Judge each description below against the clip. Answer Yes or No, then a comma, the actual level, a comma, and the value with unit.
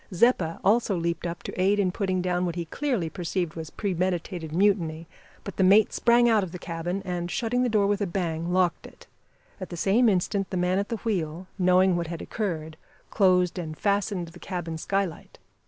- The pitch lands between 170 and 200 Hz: Yes, medium, 185 Hz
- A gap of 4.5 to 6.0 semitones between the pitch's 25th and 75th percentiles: No, average, 2.8 semitones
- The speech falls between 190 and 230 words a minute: Yes, fast, 205 wpm